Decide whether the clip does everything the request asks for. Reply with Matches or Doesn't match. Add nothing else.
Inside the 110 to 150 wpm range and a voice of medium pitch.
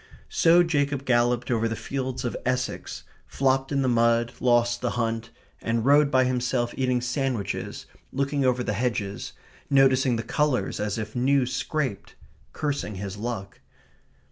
Doesn't match